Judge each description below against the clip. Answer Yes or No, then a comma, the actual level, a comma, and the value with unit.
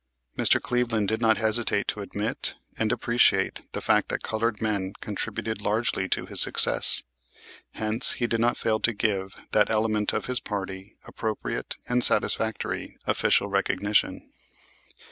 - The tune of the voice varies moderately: No, narrow, 1.9 semitones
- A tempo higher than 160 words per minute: No, average, 145 wpm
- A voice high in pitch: No, low, 110 Hz